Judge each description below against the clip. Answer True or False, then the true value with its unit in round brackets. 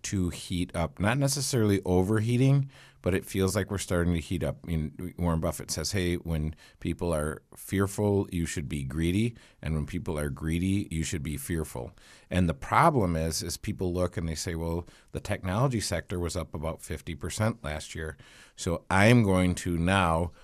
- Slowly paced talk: False (190 wpm)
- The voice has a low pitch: True (90 Hz)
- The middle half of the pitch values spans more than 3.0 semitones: True (3.5 semitones)